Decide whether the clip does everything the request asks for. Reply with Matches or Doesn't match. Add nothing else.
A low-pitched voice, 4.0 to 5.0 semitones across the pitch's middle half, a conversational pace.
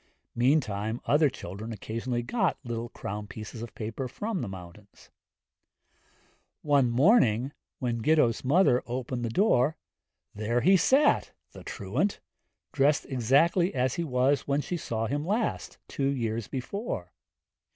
Doesn't match